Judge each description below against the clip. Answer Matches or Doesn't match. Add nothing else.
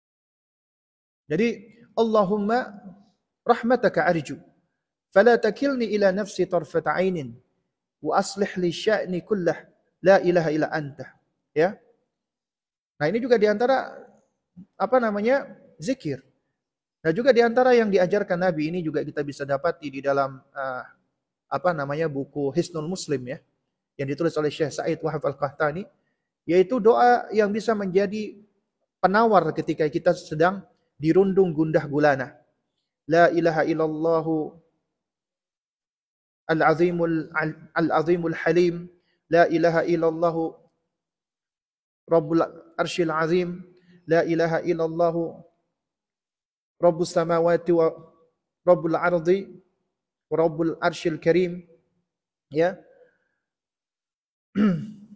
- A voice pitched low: Doesn't match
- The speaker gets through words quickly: Doesn't match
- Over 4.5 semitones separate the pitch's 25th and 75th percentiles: Doesn't match